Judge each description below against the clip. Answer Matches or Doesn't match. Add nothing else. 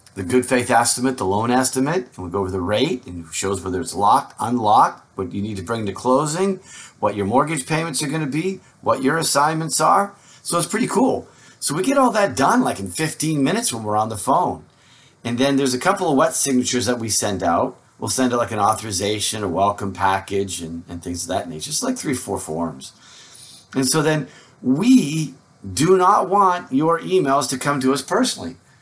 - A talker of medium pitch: Doesn't match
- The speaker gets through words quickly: Matches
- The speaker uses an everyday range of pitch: Doesn't match